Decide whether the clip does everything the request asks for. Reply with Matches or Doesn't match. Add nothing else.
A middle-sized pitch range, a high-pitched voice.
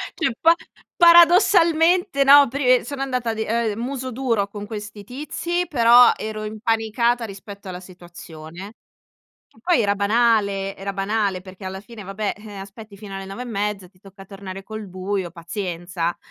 Matches